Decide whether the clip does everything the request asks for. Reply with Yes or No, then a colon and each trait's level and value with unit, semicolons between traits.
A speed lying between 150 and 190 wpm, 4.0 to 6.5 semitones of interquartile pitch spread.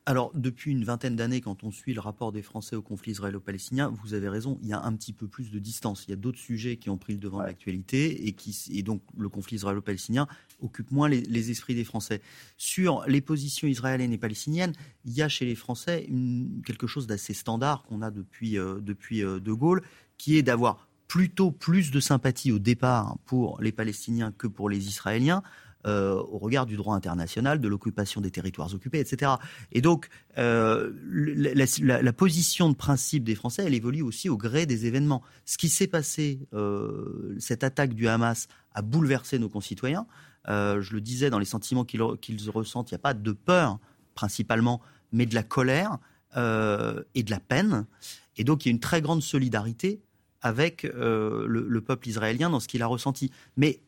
No: average, 205 wpm; average, 4.5 semitones